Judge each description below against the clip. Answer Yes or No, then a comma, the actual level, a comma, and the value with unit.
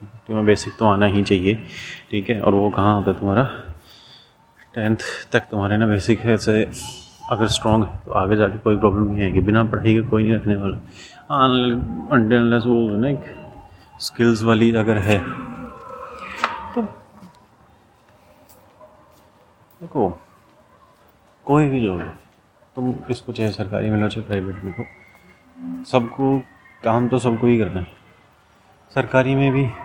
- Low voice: Yes, low, 110 Hz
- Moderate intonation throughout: Yes, average, 3.4 semitones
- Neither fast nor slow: Yes, average, 140 wpm